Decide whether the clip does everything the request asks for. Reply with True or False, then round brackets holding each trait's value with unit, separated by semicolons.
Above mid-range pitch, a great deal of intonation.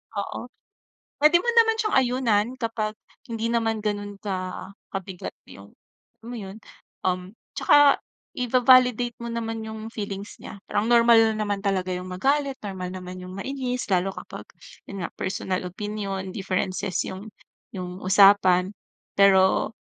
False (205 Hz; 3.7 semitones)